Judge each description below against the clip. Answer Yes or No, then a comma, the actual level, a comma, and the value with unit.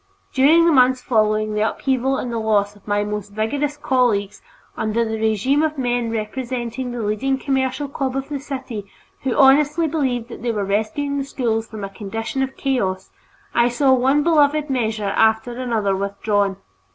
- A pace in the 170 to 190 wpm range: Yes, average, 175 wpm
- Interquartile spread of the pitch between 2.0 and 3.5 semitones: No, average, 3.9 semitones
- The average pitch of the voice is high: Yes, high, 245 Hz